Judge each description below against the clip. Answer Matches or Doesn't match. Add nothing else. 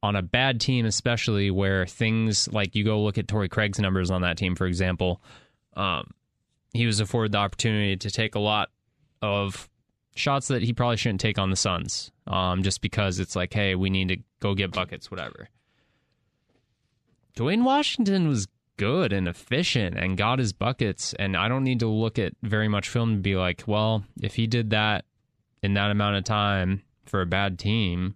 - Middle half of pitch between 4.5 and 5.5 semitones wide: Doesn't match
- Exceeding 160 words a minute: Matches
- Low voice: Matches